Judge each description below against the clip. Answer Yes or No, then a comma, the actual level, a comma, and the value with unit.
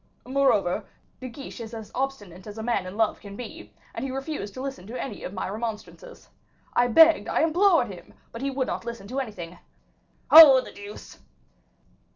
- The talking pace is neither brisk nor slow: Yes, average, 190 wpm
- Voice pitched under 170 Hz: No, high, 240 Hz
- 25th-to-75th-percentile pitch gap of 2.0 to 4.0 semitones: No, average, 4.8 semitones